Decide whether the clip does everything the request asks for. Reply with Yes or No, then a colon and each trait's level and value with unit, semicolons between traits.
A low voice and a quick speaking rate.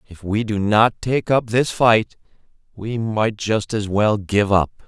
No: low, 105 Hz; average, 185 wpm